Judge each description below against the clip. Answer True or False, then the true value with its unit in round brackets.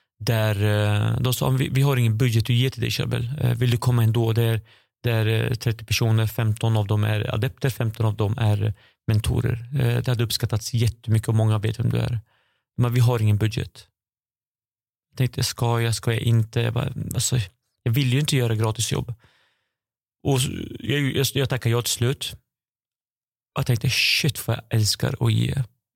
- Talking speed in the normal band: True (175 wpm)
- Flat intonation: True (2.2 semitones)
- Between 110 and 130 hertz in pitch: True (120 Hz)